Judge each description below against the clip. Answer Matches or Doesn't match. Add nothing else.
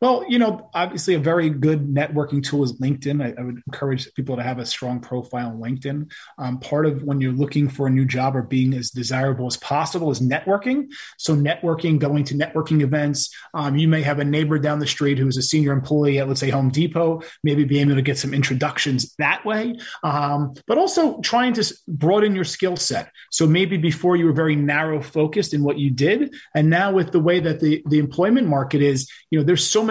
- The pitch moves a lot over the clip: Doesn't match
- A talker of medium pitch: Matches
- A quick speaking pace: Matches